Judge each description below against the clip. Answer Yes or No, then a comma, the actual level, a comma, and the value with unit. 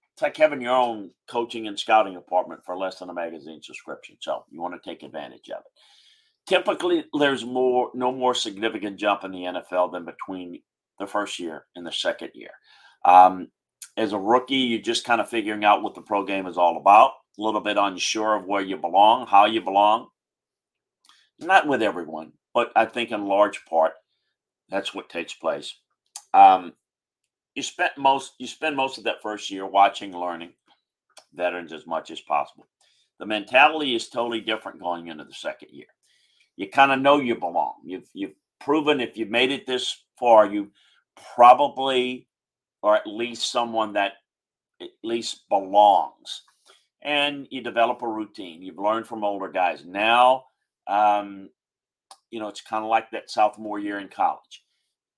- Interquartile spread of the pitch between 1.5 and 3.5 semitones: No, average, 4.3 semitones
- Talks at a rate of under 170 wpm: No, average, 175 wpm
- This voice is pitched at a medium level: No, low, 110 Hz